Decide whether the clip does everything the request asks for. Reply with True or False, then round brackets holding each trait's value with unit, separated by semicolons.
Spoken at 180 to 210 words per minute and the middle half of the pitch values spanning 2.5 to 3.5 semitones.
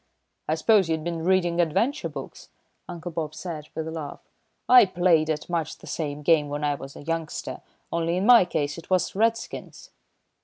True (185 wpm; 2.8 semitones)